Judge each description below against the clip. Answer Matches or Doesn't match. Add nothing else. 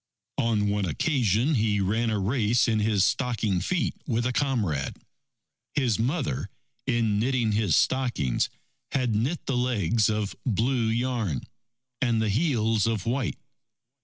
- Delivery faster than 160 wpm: Doesn't match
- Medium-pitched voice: Doesn't match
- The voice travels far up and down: Doesn't match